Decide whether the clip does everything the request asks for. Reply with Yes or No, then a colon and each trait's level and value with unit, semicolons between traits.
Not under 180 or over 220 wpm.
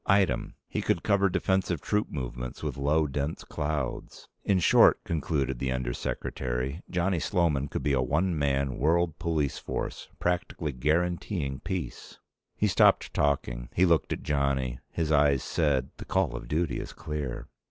No: average, 155 wpm